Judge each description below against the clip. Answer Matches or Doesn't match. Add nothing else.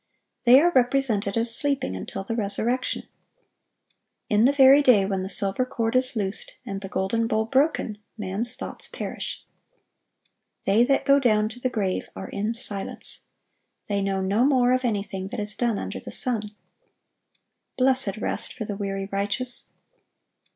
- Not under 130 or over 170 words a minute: Matches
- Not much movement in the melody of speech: Doesn't match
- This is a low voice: Doesn't match